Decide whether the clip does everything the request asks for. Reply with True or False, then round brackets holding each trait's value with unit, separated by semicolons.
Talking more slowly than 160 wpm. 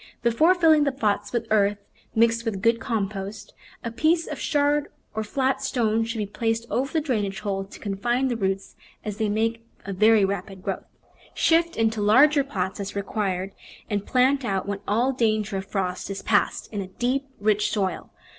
False (185 wpm)